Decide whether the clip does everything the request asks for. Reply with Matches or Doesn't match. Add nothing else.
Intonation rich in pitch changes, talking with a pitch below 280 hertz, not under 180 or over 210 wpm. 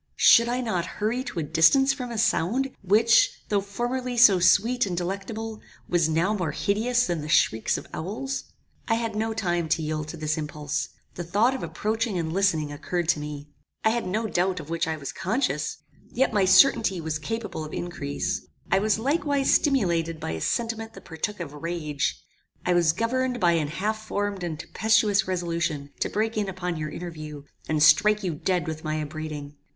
Matches